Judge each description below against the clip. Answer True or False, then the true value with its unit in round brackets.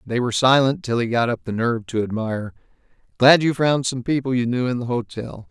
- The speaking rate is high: True (230 wpm)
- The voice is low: True (125 Hz)